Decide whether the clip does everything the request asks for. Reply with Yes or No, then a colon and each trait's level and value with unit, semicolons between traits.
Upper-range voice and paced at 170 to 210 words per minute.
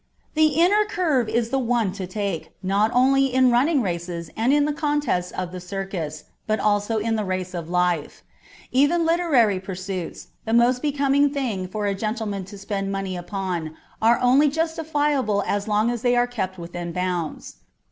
Yes: high, 215 Hz; average, 175 wpm